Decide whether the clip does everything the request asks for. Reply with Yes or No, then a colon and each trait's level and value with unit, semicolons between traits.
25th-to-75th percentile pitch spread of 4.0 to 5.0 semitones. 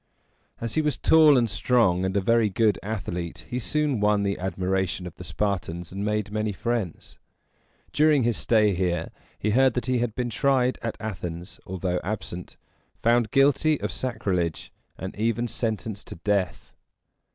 Yes: average, 4.4 semitones